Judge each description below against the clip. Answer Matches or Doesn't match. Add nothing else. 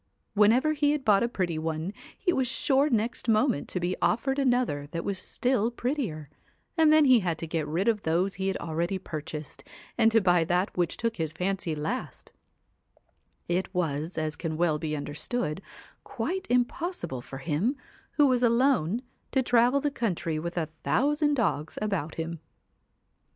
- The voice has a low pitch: Doesn't match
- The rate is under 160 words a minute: Doesn't match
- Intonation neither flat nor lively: Doesn't match